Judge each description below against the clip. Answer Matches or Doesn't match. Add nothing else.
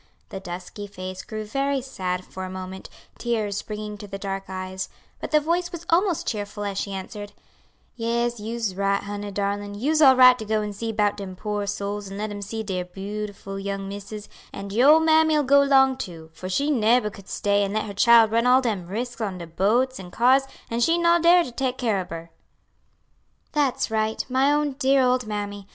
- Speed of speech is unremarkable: Doesn't match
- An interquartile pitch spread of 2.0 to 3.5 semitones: Doesn't match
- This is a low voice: Doesn't match